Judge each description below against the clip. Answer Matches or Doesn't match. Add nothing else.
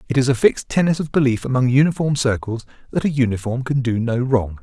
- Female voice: Doesn't match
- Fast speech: Matches